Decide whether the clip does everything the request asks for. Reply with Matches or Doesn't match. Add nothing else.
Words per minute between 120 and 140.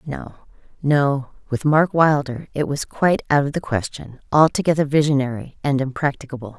Matches